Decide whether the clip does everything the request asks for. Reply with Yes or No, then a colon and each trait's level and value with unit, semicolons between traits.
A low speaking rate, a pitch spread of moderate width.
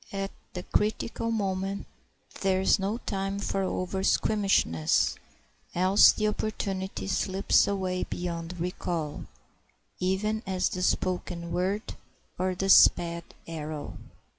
No: slow, 115 wpm; narrow, 1.8 semitones